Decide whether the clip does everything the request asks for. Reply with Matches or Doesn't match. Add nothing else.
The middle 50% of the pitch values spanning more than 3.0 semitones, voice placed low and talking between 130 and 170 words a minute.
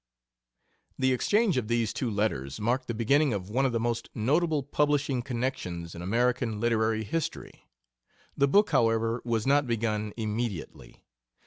Matches